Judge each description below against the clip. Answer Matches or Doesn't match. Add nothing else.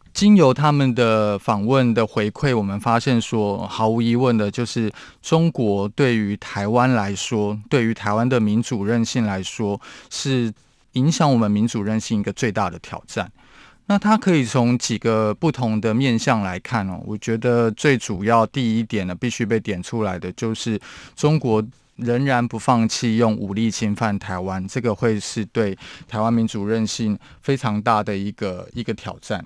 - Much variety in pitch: Doesn't match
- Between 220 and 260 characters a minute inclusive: Matches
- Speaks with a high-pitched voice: Doesn't match